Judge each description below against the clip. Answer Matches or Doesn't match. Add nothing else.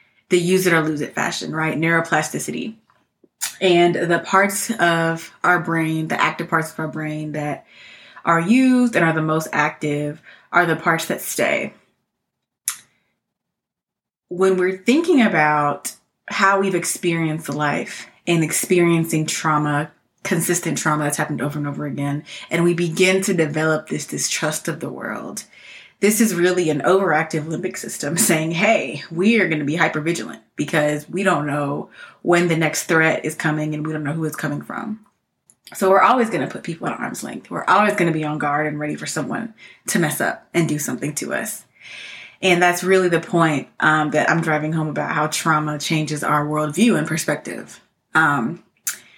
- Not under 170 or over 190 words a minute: Matches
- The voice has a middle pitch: Matches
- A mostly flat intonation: Doesn't match